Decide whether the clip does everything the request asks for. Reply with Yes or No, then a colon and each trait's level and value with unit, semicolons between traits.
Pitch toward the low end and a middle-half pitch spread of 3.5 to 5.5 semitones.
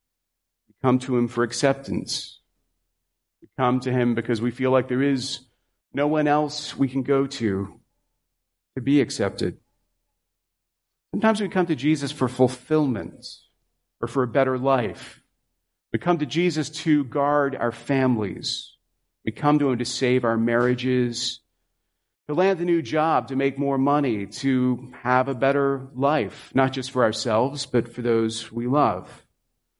No: low, 130 Hz; average, 3.0 semitones